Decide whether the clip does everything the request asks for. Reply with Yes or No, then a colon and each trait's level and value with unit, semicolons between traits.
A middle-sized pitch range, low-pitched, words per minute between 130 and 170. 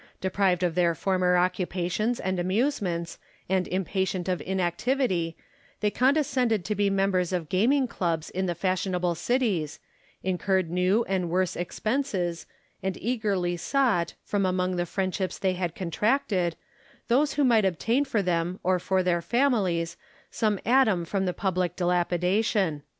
No: average, 3.3 semitones; medium, 185 Hz; average, 140 wpm